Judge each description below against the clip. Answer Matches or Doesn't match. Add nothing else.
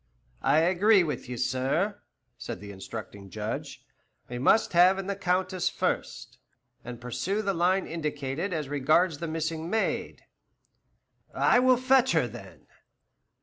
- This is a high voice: Doesn't match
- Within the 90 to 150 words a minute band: Matches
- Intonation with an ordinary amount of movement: Doesn't match